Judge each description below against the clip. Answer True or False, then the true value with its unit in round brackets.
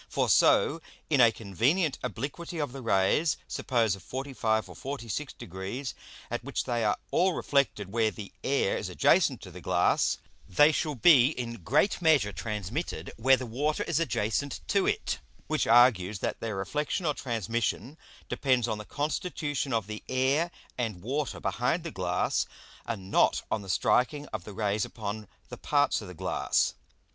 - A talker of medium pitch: False (120 Hz)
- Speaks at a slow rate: False (170 wpm)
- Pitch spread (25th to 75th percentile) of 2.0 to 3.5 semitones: False (5.6 semitones)